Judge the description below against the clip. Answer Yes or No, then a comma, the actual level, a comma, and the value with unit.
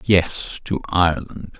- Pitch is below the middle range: Yes, very low, 90 Hz